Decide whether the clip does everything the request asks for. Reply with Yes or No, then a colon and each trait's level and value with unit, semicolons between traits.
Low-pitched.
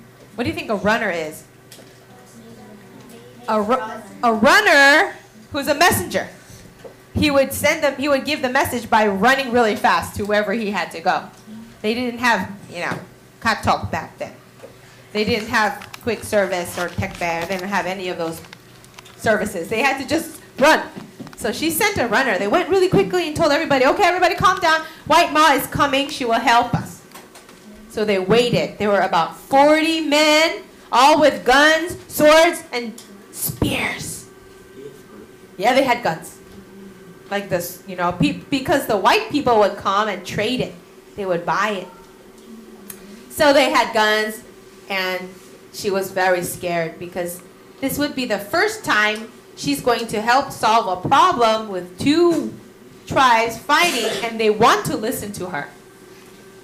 No: high, 225 Hz